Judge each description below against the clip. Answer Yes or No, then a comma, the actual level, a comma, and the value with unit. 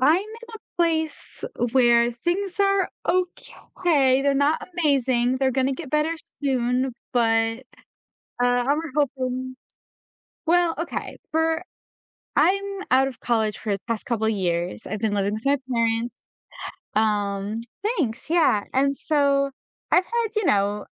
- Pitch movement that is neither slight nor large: No, wide, 5.7 semitones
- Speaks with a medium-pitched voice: No, very high, 260 Hz